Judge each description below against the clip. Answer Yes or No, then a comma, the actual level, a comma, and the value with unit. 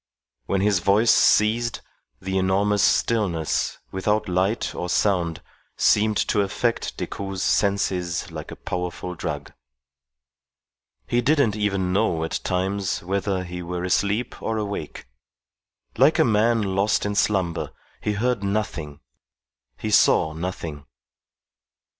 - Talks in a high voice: No, low, 100 Hz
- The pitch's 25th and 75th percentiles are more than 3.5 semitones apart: No, average, 2.8 semitones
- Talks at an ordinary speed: No, slow, 120 wpm